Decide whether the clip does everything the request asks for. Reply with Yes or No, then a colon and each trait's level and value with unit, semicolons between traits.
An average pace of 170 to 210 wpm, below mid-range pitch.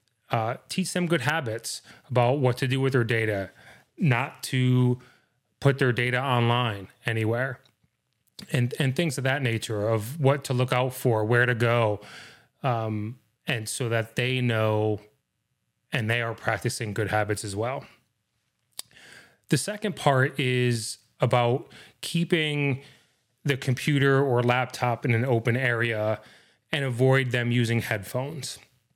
No: average, 140 wpm; low, 125 Hz